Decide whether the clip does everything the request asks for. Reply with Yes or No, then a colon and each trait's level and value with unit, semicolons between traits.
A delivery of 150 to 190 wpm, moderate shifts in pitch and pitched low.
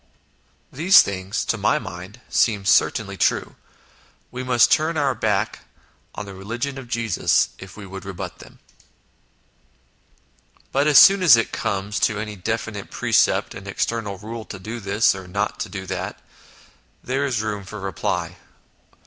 Yes: average, 155 wpm; average, 3.7 semitones; low, 105 Hz